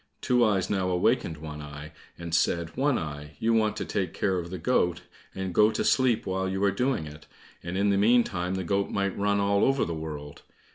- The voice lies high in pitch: No, very low, 95 Hz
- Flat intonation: No, average, 3.8 semitones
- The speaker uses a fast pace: Yes, fast, 220 wpm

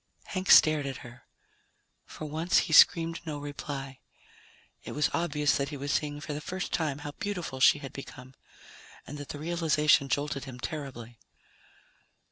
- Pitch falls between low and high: Yes, medium, 145 Hz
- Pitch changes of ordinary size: No, narrow, 2.3 semitones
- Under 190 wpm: Yes, average, 160 wpm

